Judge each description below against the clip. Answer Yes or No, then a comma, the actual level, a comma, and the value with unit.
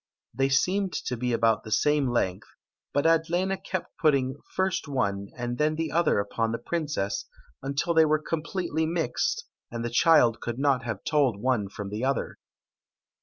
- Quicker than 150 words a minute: Yes, average, 170 wpm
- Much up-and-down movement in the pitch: Yes, wide, 5.8 semitones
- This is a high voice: No, medium, 140 Hz